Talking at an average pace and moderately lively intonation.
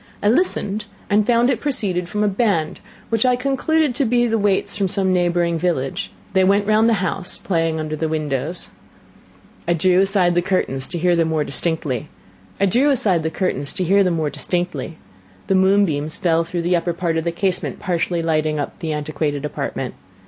Yes: average, 165 wpm; average, 3.9 semitones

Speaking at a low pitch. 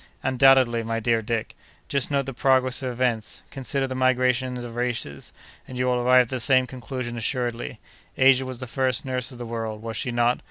Yes: low, 125 Hz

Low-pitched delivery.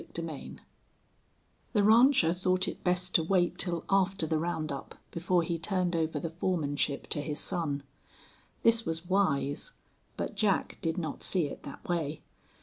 No: medium, 170 Hz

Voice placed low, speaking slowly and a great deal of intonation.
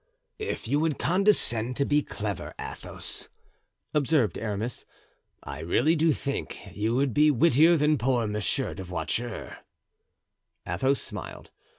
Yes: low, 130 Hz; slow, 125 wpm; wide, 5.7 semitones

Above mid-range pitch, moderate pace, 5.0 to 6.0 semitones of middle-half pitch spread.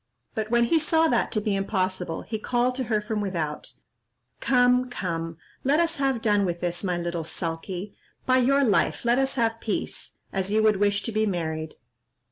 Yes: high, 215 Hz; average, 190 wpm; average, 5.3 semitones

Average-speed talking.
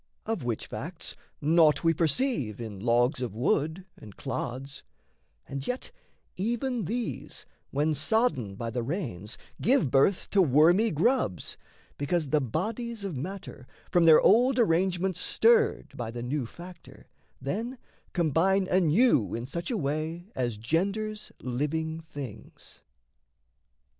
No: slow, 130 wpm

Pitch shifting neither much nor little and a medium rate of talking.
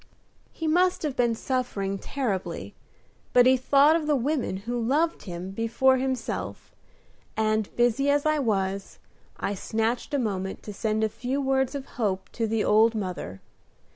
Yes: average, 4.5 semitones; average, 160 wpm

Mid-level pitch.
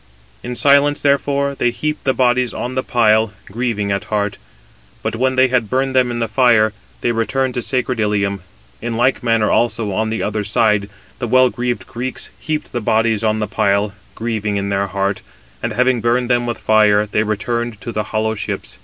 No: low, 115 Hz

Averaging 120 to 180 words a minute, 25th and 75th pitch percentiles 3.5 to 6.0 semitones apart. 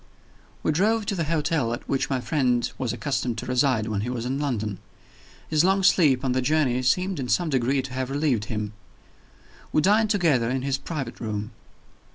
No: average, 195 wpm; average, 4.3 semitones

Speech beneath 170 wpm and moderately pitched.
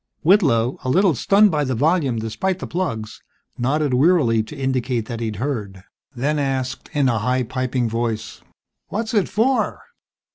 No: average, 155 wpm; low, 130 Hz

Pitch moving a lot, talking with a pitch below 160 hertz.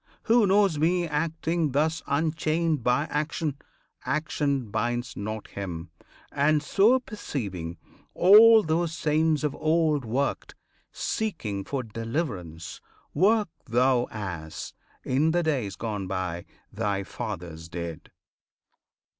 Yes: wide, 7.9 semitones; medium, 140 Hz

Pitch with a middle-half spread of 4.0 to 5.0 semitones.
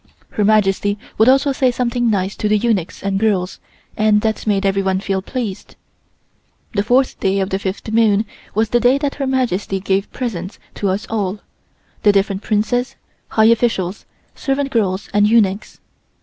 No: average, 3.2 semitones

